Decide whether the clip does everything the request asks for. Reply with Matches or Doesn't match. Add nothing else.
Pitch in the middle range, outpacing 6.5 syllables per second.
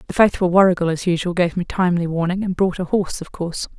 Matches